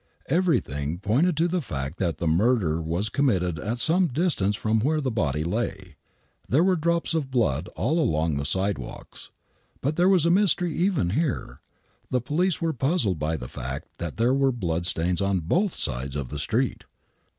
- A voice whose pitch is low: Yes, low, 110 Hz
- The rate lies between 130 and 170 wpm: No, average, 180 wpm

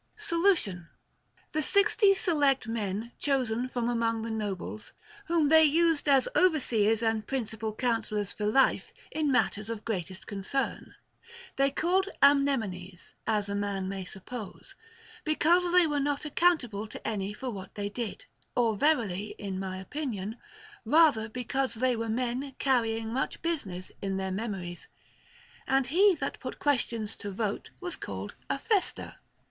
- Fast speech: No, average, 145 wpm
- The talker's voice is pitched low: No, high, 230 Hz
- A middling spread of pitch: No, wide, 5.8 semitones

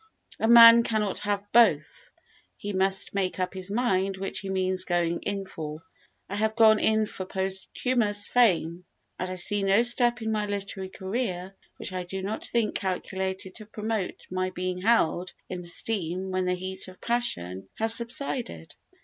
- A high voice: Yes, high, 195 Hz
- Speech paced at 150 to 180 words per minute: Yes, average, 165 wpm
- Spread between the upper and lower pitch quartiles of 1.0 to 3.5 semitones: Yes, average, 3.0 semitones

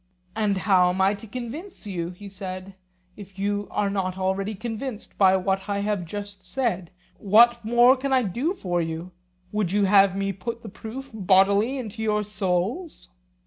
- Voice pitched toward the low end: No, high, 200 Hz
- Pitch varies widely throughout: No, average, 2.9 semitones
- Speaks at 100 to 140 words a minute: No, average, 175 wpm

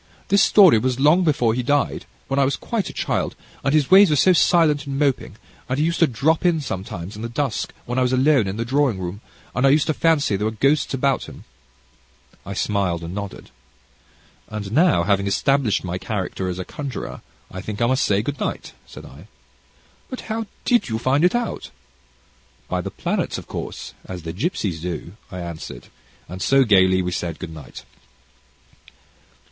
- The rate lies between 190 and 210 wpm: Yes, average, 195 wpm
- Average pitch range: No, wide, 7.3 semitones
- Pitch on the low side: Yes, low, 125 Hz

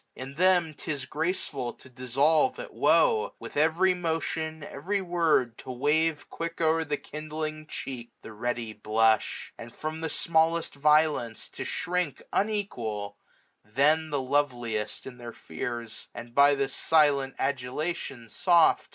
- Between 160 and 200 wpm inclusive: No, average, 140 wpm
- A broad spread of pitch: No, average, 4.9 semitones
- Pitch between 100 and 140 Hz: No, medium, 150 Hz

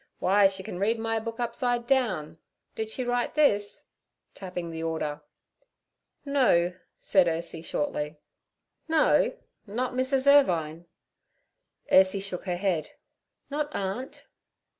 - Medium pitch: No, high, 200 Hz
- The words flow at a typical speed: No, slow, 120 wpm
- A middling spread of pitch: No, wide, 6.1 semitones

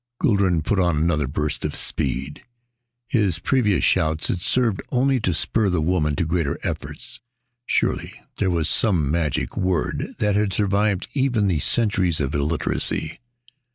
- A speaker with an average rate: Yes, average, 150 wpm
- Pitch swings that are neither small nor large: Yes, average, 5.0 semitones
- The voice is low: Yes, very low, 90 Hz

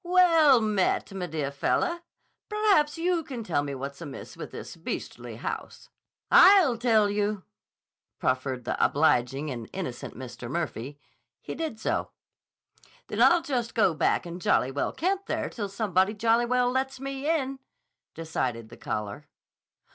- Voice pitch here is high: Yes, high, 205 Hz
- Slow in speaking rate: No, average, 145 wpm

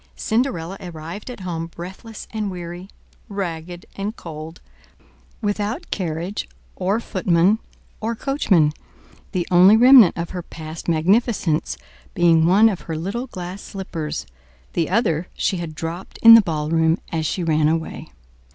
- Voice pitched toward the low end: No, medium, 175 Hz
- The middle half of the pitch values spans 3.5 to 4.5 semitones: Yes, average, 4.0 semitones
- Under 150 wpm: Yes, slow, 135 wpm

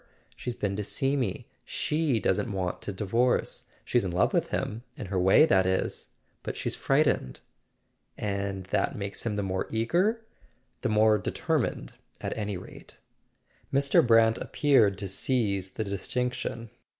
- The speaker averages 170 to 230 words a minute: No, average, 150 wpm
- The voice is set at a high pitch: No, low, 105 Hz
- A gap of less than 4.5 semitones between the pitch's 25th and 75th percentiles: Yes, average, 4.1 semitones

